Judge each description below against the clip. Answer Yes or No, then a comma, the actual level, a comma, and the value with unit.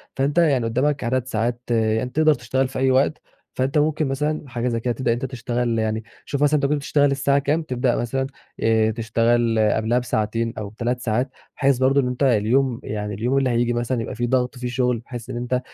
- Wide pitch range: No, average, 2.7 semitones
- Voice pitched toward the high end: No, low, 125 Hz